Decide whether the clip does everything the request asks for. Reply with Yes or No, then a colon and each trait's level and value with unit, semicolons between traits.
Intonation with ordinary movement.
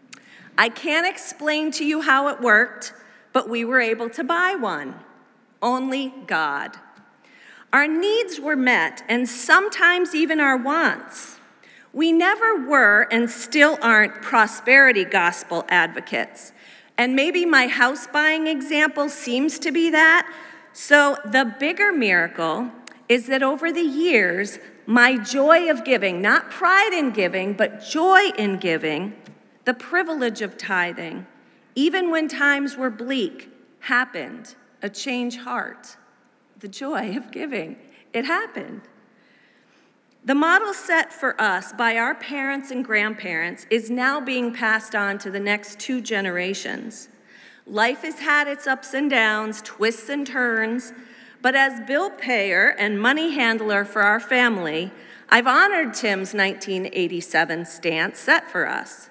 No: wide, 5.7 semitones